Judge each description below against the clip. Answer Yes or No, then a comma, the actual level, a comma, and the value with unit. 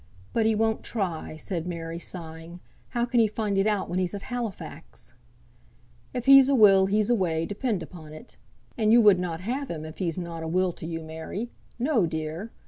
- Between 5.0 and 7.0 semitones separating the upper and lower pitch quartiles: Yes, average, 5.3 semitones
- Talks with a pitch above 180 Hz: Yes, high, 190 Hz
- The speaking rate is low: No, fast, 205 wpm